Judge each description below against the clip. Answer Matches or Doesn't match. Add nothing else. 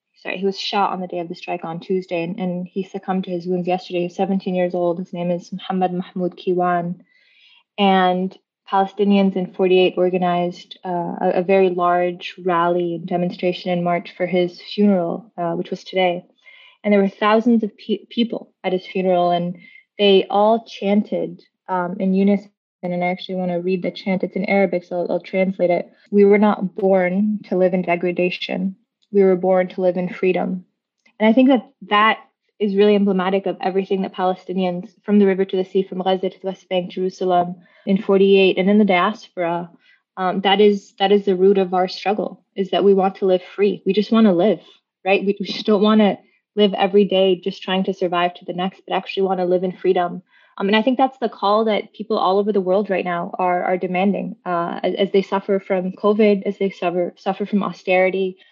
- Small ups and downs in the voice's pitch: Matches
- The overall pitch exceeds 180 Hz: Matches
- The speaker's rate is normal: Doesn't match